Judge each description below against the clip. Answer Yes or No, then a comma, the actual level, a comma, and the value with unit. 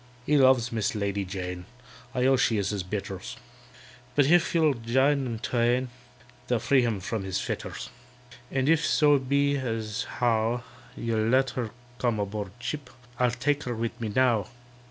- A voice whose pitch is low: Yes, low, 120 Hz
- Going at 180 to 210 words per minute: No, average, 165 wpm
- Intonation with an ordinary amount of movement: Yes, average, 3.6 semitones